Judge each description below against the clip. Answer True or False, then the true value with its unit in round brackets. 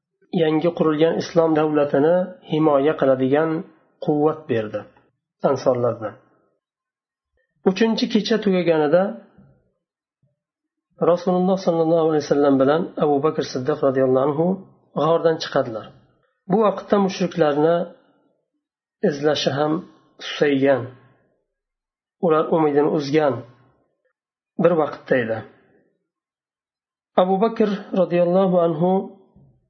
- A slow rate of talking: True (80 wpm)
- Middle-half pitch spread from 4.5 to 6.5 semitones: False (4.0 semitones)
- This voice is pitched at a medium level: True (165 Hz)